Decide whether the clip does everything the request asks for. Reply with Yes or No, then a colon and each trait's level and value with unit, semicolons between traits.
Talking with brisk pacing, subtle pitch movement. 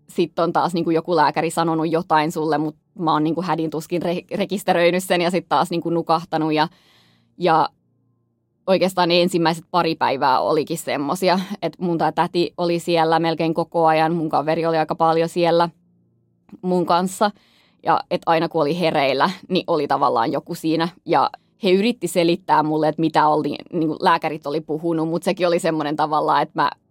Yes: fast, 175 wpm; narrow, 1.9 semitones